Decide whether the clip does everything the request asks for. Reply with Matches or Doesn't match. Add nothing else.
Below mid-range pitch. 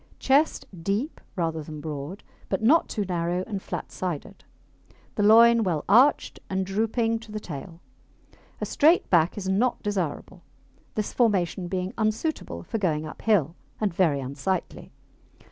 Doesn't match